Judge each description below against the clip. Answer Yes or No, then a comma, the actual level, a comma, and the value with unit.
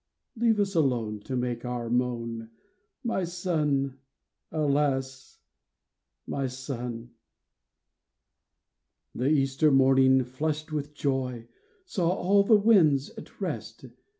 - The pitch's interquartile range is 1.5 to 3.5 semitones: No, average, 4.0 semitones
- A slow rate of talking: Yes, slow, 110 wpm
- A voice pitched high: No, low, 135 Hz